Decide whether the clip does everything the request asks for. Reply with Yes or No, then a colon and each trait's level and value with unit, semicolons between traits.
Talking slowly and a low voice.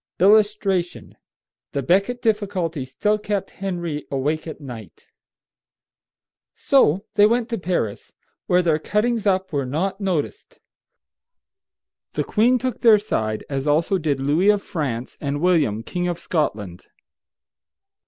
No: slow, 125 wpm; medium, 180 Hz